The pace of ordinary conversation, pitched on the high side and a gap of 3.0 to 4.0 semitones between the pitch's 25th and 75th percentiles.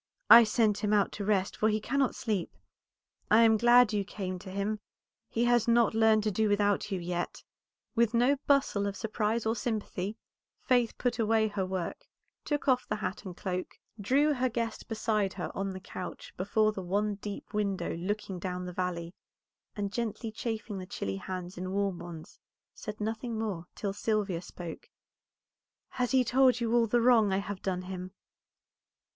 Yes: average, 180 wpm; high, 210 Hz; average, 3.3 semitones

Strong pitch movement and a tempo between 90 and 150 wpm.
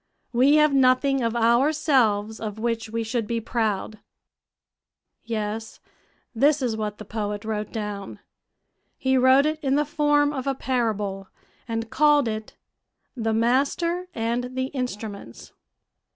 No: average, 3.8 semitones; slow, 135 wpm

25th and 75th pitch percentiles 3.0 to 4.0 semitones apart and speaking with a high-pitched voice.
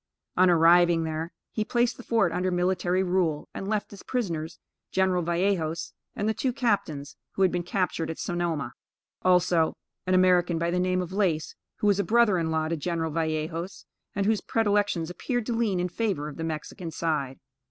No: average, 3.4 semitones; medium, 180 Hz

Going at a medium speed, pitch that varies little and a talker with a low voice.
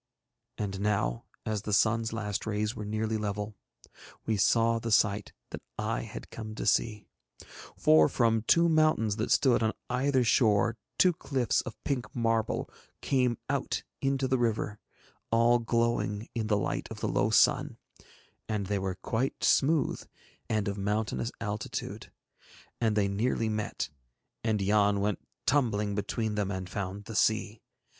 Yes: average, 150 wpm; narrow, 2.2 semitones; low, 110 Hz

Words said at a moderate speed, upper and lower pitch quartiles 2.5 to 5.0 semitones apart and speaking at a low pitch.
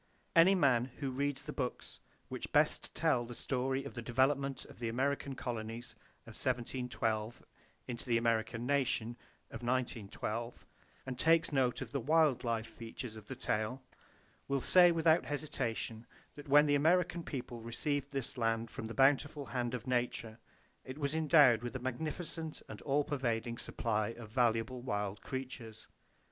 Yes: average, 160 wpm; average, 3.5 semitones; low, 125 Hz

